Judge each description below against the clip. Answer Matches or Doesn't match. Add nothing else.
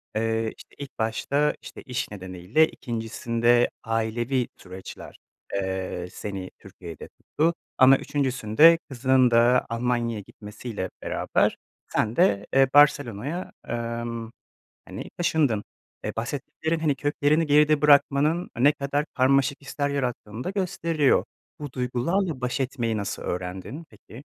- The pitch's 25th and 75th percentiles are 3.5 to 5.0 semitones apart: Matches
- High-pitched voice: Doesn't match